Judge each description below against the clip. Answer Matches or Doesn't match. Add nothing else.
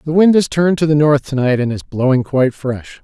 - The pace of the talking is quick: Matches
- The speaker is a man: Matches